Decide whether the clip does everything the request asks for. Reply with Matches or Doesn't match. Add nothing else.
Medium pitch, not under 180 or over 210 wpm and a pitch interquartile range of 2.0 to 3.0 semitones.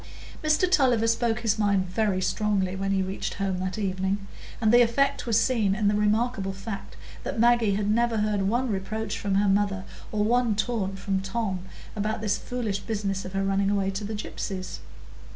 Doesn't match